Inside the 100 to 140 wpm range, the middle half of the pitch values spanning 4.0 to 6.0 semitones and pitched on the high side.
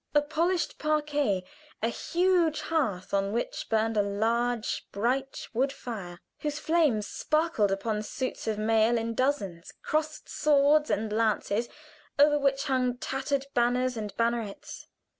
Yes: slow, 135 wpm; wide, 5.4 semitones; high, 245 Hz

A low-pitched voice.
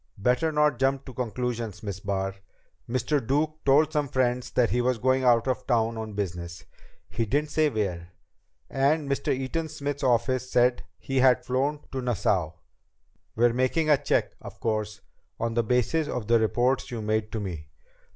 Yes: low, 125 Hz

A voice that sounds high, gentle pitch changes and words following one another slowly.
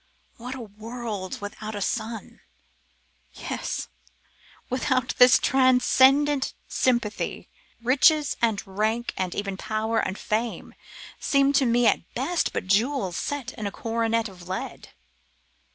No: high, 230 Hz; average, 3.7 semitones; slow, 120 wpm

